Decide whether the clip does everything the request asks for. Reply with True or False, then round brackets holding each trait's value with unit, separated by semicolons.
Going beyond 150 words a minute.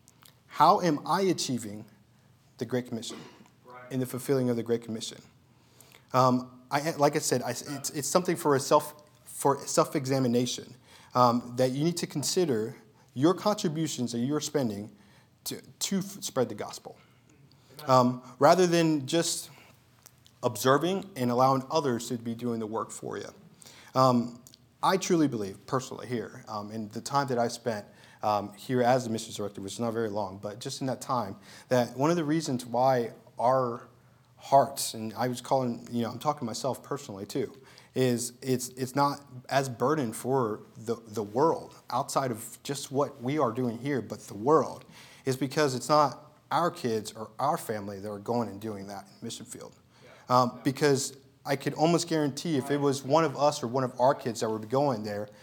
True (185 wpm)